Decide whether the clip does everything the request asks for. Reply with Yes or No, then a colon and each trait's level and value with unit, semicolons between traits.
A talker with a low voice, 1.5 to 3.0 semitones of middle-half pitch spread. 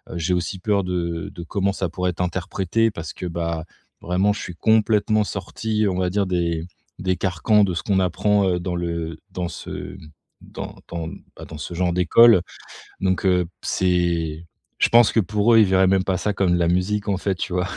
Yes: very low, 90 Hz; narrow, 2.6 semitones